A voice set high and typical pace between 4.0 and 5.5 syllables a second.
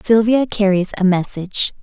Yes: high, 200 Hz; 5.0 syllables/s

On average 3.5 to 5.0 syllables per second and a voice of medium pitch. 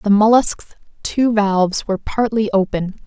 No: 4.5 syllables/s; high, 210 Hz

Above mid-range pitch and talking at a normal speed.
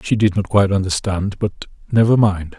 No: low, 100 Hz; average, 160 wpm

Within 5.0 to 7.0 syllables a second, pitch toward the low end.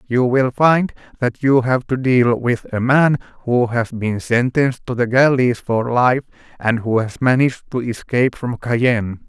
No: 4.4 syllables/s; low, 125 Hz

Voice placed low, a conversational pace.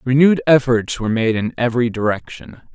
Yes: low, 125 Hz; average, 155 wpm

